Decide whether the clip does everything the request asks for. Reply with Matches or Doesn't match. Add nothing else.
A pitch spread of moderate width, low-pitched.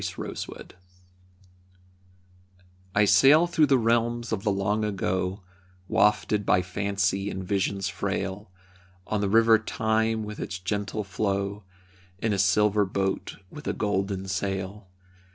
Doesn't match